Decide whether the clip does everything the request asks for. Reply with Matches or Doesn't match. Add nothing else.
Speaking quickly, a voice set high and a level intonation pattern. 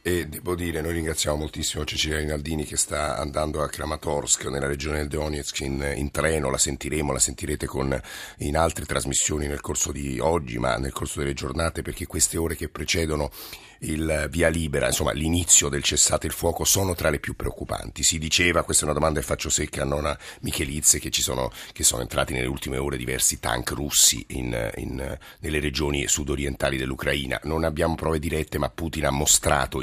Doesn't match